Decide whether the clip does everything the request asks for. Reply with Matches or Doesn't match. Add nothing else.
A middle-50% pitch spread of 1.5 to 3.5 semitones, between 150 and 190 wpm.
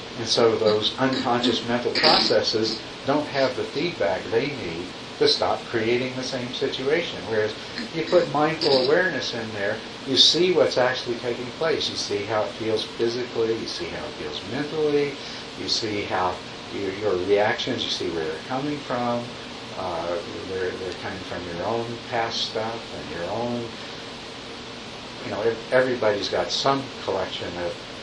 Matches